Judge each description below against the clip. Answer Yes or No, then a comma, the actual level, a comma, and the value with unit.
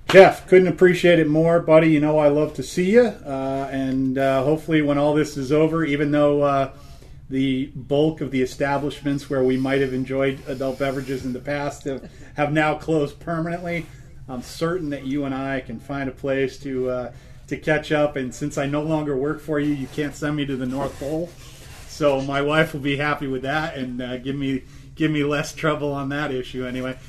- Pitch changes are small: Yes, narrow, 2.1 semitones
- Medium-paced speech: No, fast, 215 wpm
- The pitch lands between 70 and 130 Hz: No, medium, 140 Hz